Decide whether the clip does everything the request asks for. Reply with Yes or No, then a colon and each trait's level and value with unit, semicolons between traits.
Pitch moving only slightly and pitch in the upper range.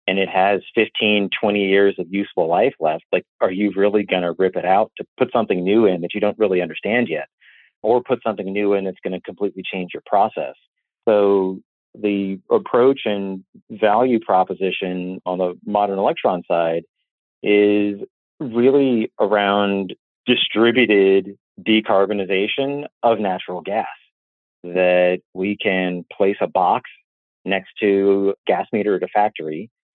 No: narrow, 1.9 semitones; low, 100 Hz